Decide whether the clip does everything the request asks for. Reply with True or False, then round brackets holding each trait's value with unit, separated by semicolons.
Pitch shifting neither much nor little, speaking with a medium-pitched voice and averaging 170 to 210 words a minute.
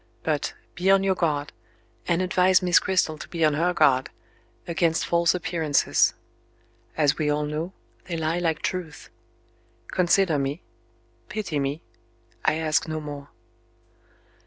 False (3.1 semitones; 160 Hz; 135 wpm)